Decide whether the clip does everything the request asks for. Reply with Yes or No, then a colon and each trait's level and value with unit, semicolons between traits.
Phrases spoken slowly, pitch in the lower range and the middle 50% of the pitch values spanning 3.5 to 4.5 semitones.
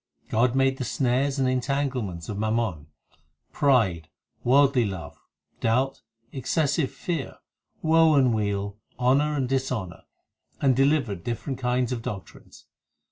Yes: slow, 120 wpm; low, 125 Hz; average, 4.0 semitones